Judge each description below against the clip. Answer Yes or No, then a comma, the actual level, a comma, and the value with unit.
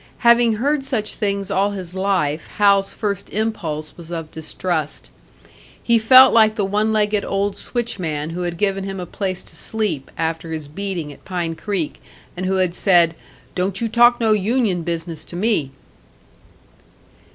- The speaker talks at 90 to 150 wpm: No, average, 165 wpm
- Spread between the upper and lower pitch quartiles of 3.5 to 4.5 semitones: Yes, average, 4.2 semitones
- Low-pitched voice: No, high, 195 Hz